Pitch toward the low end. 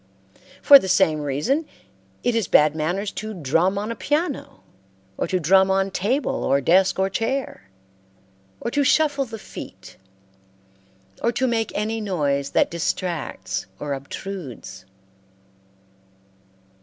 No: high, 190 Hz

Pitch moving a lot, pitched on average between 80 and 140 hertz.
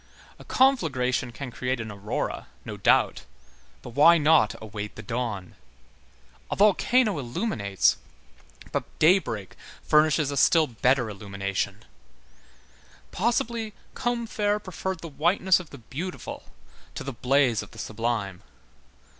Yes: wide, 8.7 semitones; low, 135 Hz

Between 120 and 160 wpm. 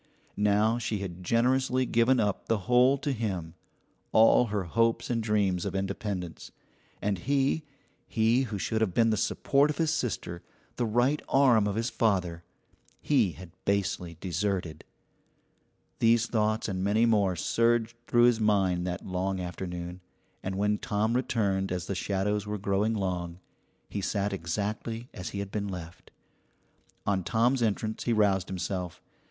Yes: average, 155 wpm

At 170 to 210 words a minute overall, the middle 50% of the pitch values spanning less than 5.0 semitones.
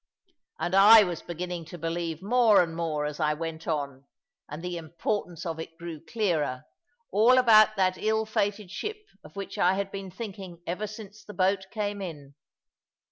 Yes: average, 175 wpm; average, 4.1 semitones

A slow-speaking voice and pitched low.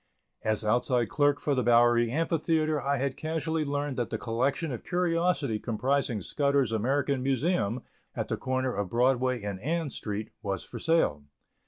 No: average, 160 wpm; low, 130 Hz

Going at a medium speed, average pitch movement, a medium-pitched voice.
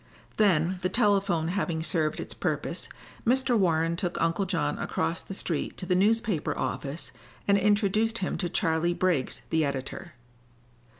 Yes: average, 145 wpm; average, 3.7 semitones; medium, 180 Hz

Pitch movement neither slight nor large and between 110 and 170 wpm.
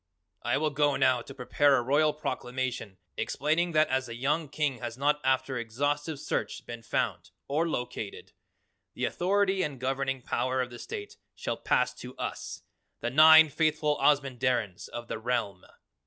Yes: average, 3.6 semitones; average, 160 wpm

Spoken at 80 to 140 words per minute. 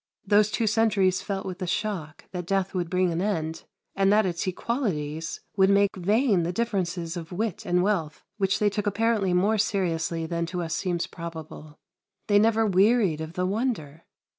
No: average, 180 wpm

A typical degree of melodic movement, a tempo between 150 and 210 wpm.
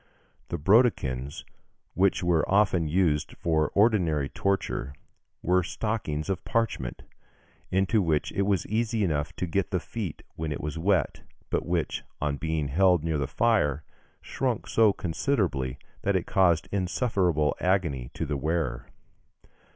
No: average, 4.7 semitones; average, 140 wpm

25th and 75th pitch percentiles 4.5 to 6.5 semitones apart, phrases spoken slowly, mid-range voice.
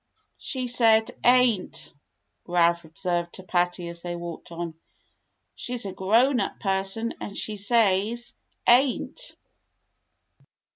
No: average, 5.2 semitones; slow, 115 wpm; high, 195 Hz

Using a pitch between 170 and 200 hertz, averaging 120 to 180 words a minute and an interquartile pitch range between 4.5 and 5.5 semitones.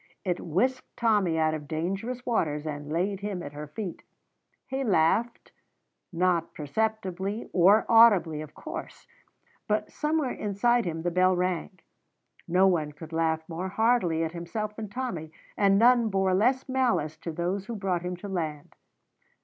Yes: medium, 185 Hz; average, 155 wpm; average, 5.1 semitones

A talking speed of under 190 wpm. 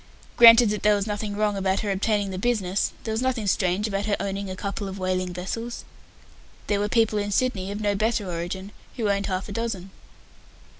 No: fast, 205 wpm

